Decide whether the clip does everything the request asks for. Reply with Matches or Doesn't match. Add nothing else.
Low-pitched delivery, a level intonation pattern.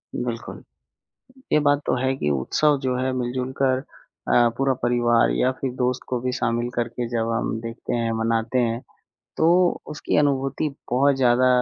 Matches